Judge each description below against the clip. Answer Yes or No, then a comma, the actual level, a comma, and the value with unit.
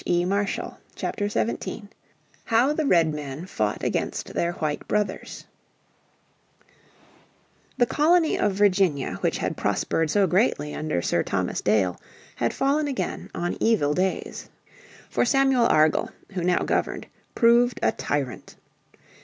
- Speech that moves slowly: Yes, slow, 120 wpm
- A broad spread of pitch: Yes, wide, 7.5 semitones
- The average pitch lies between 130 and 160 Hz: No, high, 190 Hz